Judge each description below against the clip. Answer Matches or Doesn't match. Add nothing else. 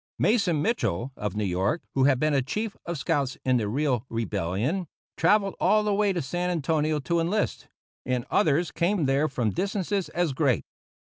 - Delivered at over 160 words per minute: Matches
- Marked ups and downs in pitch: Matches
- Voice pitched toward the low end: Doesn't match